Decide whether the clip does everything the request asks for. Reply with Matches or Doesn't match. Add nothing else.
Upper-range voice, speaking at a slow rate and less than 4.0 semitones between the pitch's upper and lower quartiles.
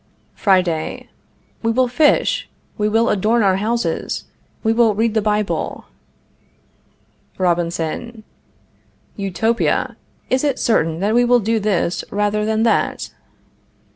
Matches